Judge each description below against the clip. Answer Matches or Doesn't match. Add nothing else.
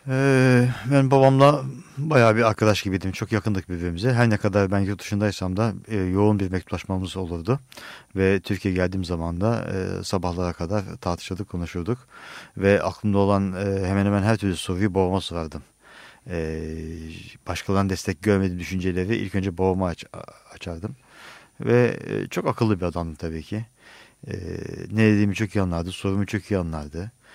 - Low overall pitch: Matches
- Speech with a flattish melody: Doesn't match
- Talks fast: Matches